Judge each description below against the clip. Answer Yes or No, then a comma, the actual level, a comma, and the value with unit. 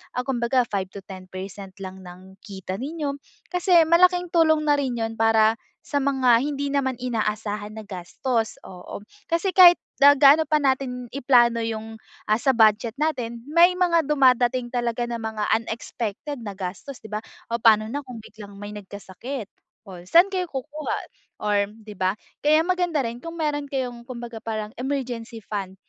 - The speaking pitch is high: Yes, high, 240 Hz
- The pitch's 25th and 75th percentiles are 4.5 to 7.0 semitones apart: Yes, average, 5.1 semitones